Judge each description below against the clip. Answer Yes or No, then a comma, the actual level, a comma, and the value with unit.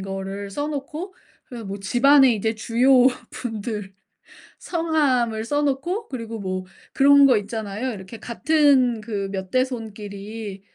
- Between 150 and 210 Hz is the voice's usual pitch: No, high, 230 Hz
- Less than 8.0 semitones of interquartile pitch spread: Yes, average, 5.2 semitones